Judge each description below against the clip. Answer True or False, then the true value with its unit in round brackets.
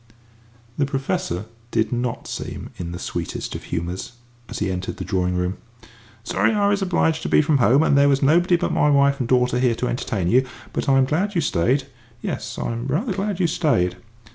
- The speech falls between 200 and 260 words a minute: True (205 wpm)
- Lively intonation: True (6.0 semitones)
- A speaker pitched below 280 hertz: True (135 Hz)